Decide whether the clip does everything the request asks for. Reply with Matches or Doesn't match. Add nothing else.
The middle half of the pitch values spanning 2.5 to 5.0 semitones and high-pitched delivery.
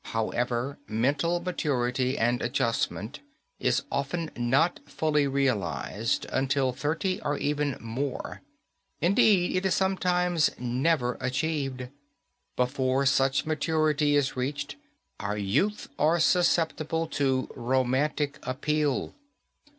Doesn't match